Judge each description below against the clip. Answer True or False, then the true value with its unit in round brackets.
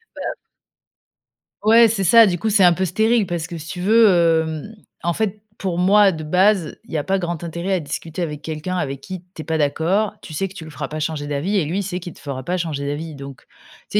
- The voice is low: False (175 Hz)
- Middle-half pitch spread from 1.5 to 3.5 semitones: False (3.9 semitones)